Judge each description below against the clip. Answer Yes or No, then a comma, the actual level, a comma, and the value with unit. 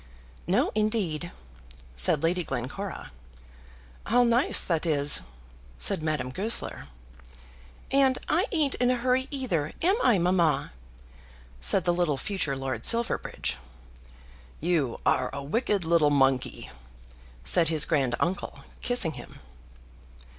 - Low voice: No, medium, 170 Hz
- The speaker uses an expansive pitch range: Yes, wide, 8.3 semitones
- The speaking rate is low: Yes, slow, 120 wpm